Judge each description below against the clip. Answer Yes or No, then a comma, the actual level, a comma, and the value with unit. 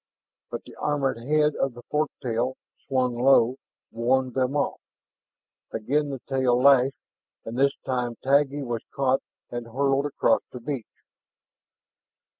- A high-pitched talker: No, low, 130 Hz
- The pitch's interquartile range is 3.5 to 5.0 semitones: No, narrow, 2.4 semitones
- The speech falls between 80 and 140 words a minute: Yes, slow, 135 wpm